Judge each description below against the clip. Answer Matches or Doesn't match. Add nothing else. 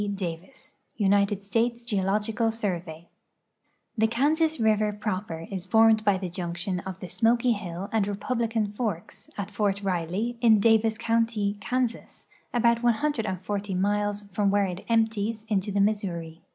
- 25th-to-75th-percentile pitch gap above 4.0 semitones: Doesn't match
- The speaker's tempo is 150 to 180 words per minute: Doesn't match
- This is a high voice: Matches